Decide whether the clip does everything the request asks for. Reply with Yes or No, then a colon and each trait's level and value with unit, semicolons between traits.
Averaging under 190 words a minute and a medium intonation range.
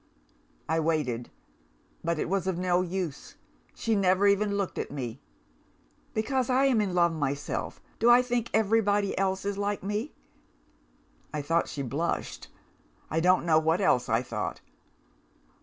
Yes: average, 150 wpm; average, 4.7 semitones